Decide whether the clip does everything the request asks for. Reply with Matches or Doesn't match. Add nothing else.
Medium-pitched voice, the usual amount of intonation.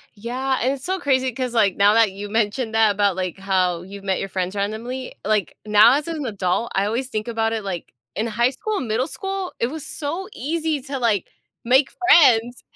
Doesn't match